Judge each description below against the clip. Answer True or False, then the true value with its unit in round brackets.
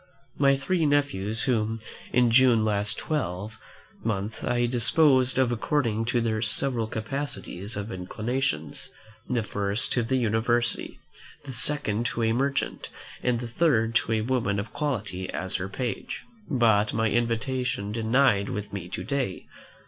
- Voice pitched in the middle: False (115 Hz)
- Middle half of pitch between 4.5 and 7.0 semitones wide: False (3.6 semitones)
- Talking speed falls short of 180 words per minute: True (145 wpm)